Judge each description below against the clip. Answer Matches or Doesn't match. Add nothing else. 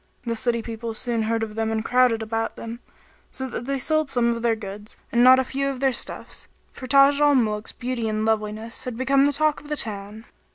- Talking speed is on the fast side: Matches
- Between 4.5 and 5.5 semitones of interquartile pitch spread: Doesn't match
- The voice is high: Matches